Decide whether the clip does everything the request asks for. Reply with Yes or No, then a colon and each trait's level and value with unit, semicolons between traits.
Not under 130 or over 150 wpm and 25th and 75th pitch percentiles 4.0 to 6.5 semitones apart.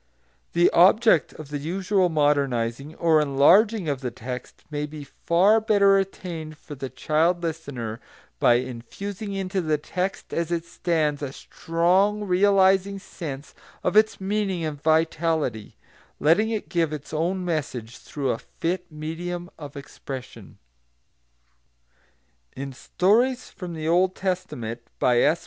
Yes: slow, 135 wpm; average, 4.6 semitones